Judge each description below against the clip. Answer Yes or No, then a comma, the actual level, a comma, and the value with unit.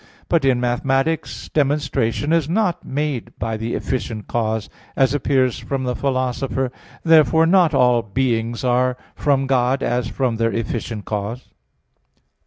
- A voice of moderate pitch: No, low, 130 Hz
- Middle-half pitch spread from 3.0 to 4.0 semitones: Yes, average, 3.3 semitones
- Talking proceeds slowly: No, average, 155 wpm